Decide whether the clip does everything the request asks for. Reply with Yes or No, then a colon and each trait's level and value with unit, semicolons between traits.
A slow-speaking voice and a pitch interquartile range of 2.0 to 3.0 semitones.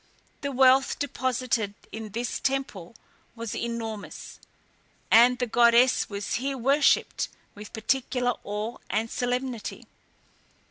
Yes: slow, 105 wpm; average, 2.7 semitones